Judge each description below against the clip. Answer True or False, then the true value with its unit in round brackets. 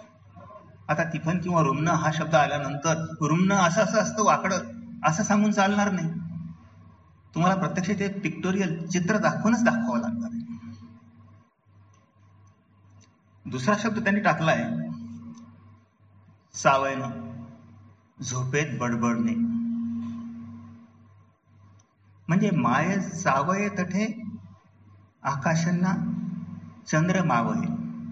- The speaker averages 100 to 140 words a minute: False (85 wpm)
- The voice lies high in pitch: False (160 Hz)